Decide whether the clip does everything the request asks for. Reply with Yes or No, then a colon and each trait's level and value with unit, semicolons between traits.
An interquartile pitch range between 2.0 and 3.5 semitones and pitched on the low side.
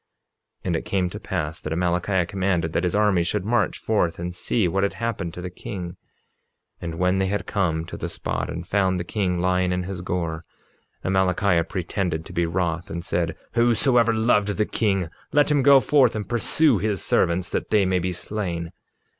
Yes: average, 3.2 semitones; very low, 90 Hz